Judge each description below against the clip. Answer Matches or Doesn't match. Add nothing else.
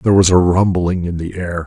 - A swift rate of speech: Matches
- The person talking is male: Matches